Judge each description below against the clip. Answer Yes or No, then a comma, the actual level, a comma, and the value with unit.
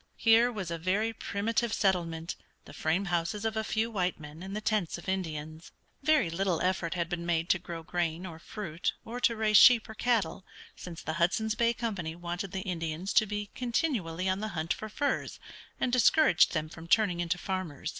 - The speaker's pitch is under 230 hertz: Yes, medium, 185 Hz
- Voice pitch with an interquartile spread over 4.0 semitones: Yes, average, 4.6 semitones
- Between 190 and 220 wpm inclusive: Yes, average, 195 wpm